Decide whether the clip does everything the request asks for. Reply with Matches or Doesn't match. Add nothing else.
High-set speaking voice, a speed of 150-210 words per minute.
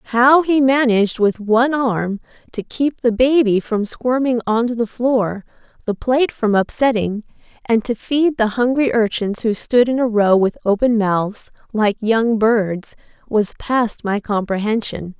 Matches